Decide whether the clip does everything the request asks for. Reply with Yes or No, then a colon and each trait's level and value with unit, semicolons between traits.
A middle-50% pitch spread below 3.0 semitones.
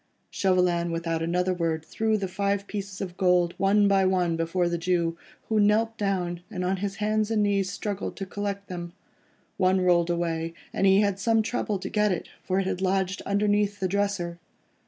Yes: narrow, 2.5 semitones